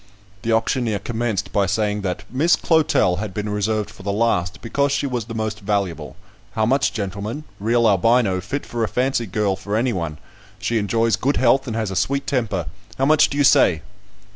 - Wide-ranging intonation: No, average, 3.6 semitones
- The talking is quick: No, average, 195 wpm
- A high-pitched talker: No, low, 110 Hz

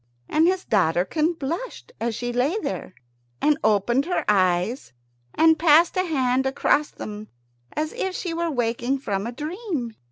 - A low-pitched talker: No, very high, 270 Hz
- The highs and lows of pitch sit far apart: Yes, wide, 6.2 semitones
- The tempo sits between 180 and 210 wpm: No, average, 155 wpm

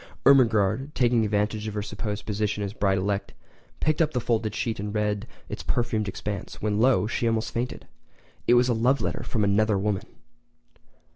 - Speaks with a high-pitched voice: No, low, 110 Hz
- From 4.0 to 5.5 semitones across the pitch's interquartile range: No, narrow, 2.5 semitones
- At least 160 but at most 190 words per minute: Yes, average, 180 wpm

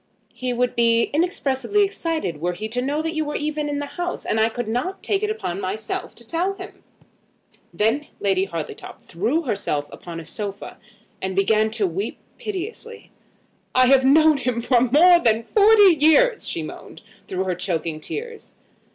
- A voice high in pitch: Yes, very high, 255 Hz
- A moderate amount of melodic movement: No, wide, 8.2 semitones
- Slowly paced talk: No, average, 175 wpm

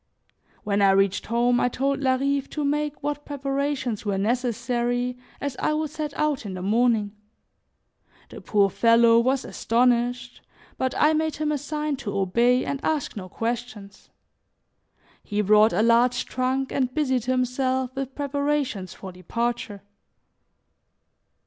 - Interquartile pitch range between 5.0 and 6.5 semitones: No, average, 3.5 semitones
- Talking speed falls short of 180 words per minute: Yes, average, 140 wpm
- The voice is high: Yes, very high, 250 Hz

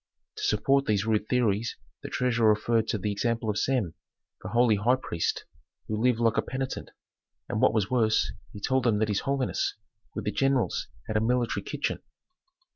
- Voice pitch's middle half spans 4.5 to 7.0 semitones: No, average, 2.9 semitones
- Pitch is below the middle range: Yes, low, 115 Hz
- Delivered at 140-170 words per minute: No, average, 185 wpm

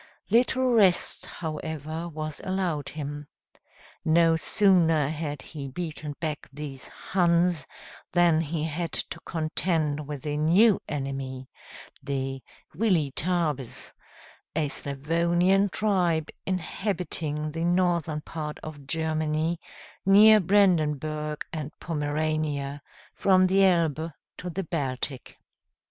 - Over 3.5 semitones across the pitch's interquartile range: No, average, 2.9 semitones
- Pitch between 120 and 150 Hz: No, medium, 160 Hz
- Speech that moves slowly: Yes, slow, 100 wpm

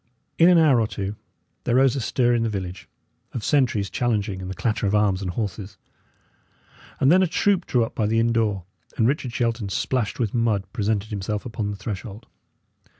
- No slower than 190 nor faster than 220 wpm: Yes, average, 200 wpm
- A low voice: Yes, low, 110 Hz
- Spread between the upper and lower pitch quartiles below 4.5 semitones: Yes, average, 3.3 semitones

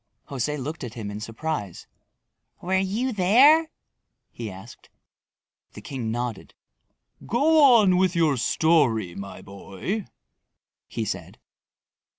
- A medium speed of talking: No, slow, 115 wpm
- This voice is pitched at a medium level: Yes, medium, 150 Hz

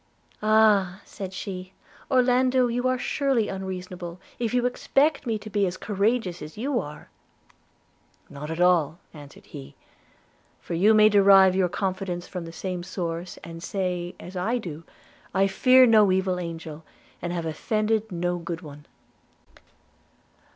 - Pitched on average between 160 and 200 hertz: Yes, high, 190 Hz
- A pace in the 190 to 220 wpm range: No, average, 145 wpm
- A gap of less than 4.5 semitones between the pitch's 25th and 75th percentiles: Yes, average, 3.9 semitones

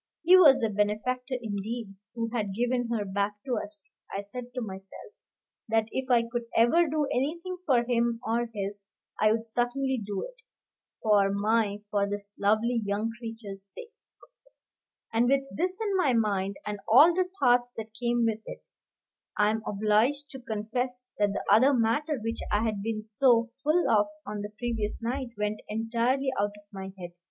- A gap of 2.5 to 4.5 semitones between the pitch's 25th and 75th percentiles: Yes, average, 3.4 semitones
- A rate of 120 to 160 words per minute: No, average, 175 wpm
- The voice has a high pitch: Yes, high, 230 Hz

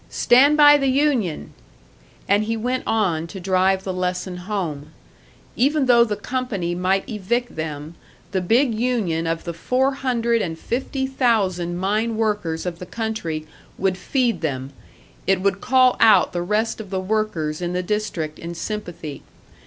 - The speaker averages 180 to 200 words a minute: No, average, 160 wpm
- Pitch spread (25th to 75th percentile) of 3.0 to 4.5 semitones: No, average, 5.3 semitones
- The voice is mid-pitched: No, high, 200 Hz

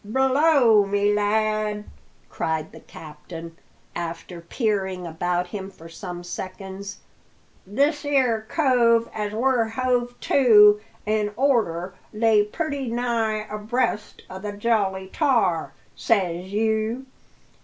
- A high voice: Yes, high, 210 Hz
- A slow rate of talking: Yes, slow, 110 wpm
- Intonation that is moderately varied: Yes, average, 3.9 semitones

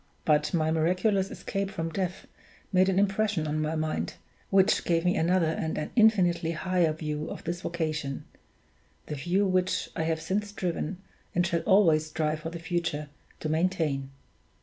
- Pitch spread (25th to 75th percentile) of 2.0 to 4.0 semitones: Yes, average, 3.1 semitones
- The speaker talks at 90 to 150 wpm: No, average, 165 wpm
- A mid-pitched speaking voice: Yes, medium, 170 Hz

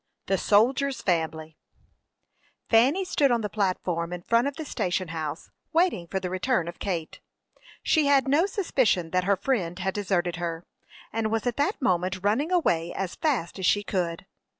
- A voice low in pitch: No, high, 195 Hz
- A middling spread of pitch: No, wide, 7.1 semitones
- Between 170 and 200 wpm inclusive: Yes, average, 175 wpm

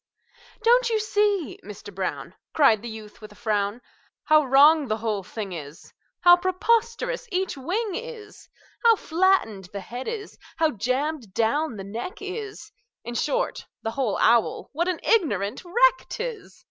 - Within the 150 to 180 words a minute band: Yes, average, 160 wpm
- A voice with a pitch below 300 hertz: No, very high, 305 Hz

